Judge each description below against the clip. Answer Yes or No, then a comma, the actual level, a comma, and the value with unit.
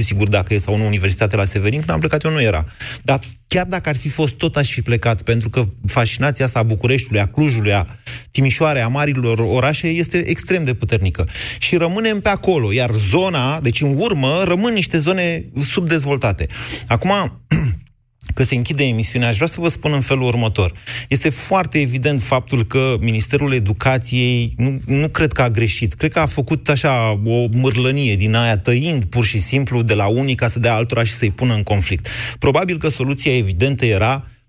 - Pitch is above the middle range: No, low, 125 Hz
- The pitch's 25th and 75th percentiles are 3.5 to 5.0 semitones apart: Yes, average, 4.4 semitones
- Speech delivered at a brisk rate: Yes, fast, 190 wpm